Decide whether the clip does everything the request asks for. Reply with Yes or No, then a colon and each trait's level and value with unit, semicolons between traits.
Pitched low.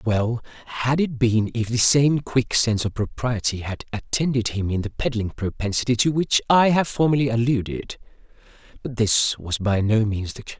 Yes: low, 120 Hz